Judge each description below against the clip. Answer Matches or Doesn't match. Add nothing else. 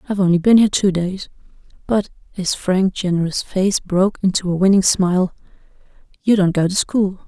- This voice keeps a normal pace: Matches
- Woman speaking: Matches